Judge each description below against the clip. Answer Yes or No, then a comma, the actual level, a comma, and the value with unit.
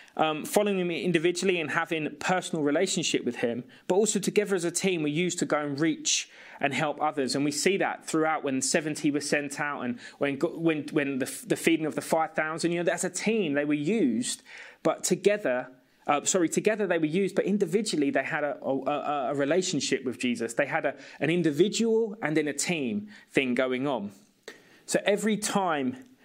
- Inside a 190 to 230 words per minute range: Yes, average, 200 wpm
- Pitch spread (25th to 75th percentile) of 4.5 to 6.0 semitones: Yes, average, 5.3 semitones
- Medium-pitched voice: Yes, medium, 165 Hz